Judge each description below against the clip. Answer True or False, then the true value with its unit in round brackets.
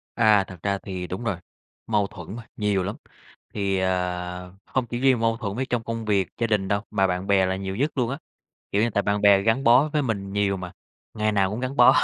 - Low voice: True (100 Hz)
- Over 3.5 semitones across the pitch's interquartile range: False (3.2 semitones)